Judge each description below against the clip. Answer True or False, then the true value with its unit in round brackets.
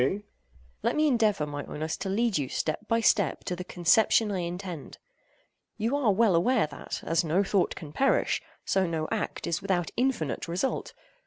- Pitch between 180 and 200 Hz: True (190 Hz)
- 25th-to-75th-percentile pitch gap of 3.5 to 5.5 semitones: True (5.1 semitones)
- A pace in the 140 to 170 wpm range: False (180 wpm)